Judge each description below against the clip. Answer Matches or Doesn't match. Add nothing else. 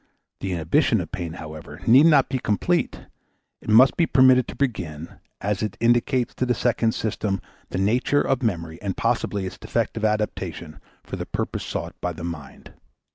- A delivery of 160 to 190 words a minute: Matches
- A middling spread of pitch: Doesn't match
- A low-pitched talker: Matches